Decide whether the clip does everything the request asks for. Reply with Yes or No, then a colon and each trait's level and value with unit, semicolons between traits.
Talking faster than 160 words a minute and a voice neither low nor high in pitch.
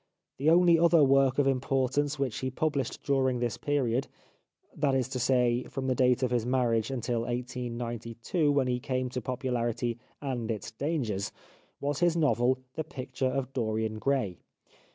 No: average, 175 wpm; low, 130 Hz